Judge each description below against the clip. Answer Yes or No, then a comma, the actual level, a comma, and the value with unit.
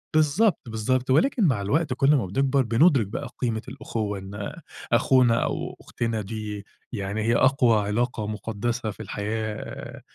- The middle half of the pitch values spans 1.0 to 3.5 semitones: No, average, 3.9 semitones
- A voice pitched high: No, low, 115 Hz